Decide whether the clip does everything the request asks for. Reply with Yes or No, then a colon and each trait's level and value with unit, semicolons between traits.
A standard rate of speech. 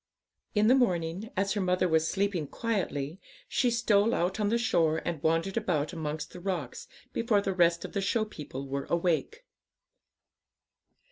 Yes: average, 160 wpm